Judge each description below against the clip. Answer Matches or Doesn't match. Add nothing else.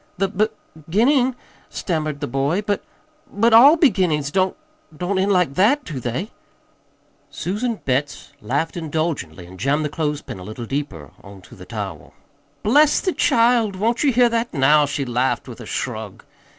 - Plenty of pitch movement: Matches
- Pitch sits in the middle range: Matches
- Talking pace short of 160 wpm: Doesn't match